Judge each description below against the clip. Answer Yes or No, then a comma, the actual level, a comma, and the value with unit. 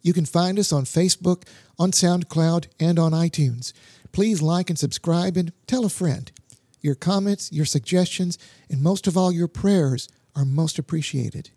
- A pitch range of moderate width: Yes, average, 3.9 semitones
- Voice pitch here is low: No, medium, 165 Hz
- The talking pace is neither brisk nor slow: Yes, average, 165 wpm